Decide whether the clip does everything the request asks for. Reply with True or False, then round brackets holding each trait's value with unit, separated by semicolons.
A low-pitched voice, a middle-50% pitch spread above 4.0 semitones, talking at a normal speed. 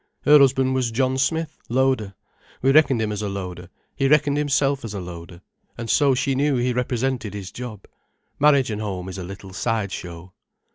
True (120 Hz; 5.5 semitones; 190 wpm)